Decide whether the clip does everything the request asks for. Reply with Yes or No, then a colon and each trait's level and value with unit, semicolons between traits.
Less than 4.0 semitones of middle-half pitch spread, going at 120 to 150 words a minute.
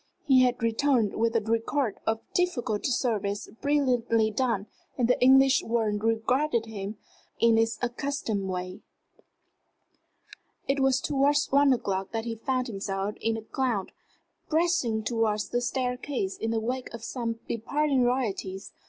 Yes: average, 3.2 semitones; average, 140 wpm